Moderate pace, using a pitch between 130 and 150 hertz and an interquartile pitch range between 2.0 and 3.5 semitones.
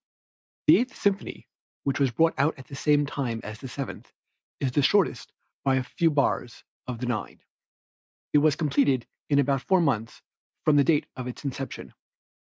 Yes: average, 180 wpm; medium, 140 Hz; average, 2.8 semitones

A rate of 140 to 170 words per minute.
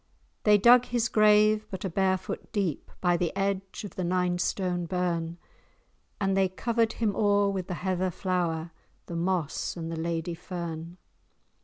Yes: average, 160 wpm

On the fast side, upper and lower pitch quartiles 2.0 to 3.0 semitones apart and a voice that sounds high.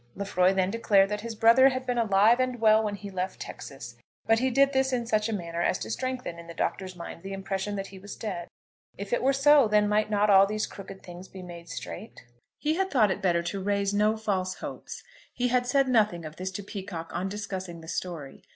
No: fast, 235 wpm; average, 3.6 semitones; high, 205 Hz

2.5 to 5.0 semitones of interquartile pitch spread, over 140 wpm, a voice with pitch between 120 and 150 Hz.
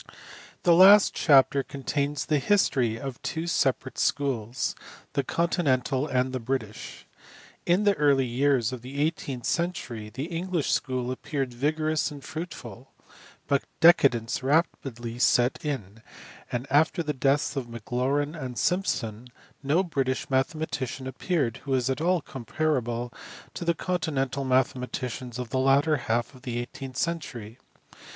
No: average, 3.7 semitones; slow, 135 wpm; low, 135 Hz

